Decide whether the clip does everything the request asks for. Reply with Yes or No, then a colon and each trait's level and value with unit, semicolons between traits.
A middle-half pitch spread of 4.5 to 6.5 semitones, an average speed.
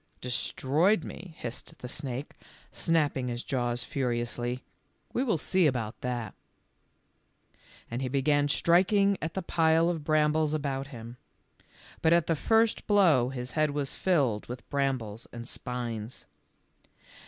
No: average, 4.8 semitones; slow, 130 wpm